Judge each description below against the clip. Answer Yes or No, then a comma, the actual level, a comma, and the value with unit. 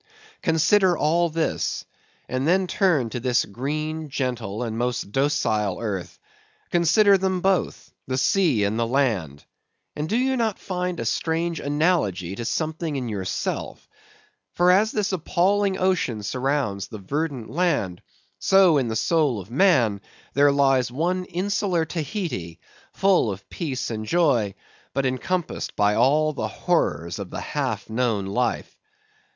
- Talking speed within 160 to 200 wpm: No, average, 145 wpm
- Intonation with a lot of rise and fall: Yes, wide, 7.6 semitones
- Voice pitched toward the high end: No, medium, 145 Hz